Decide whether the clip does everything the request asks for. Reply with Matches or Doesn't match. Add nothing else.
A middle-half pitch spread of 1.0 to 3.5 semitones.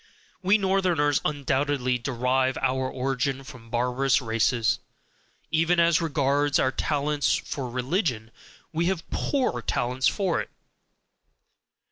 Doesn't match